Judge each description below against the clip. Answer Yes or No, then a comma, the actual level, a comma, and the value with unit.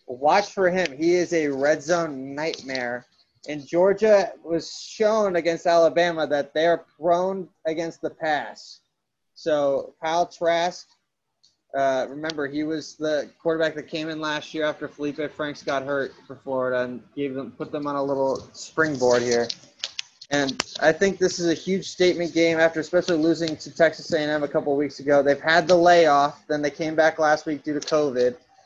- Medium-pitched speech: Yes, medium, 155 Hz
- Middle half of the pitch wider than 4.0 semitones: No, average, 2.8 semitones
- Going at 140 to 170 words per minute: No, average, 180 wpm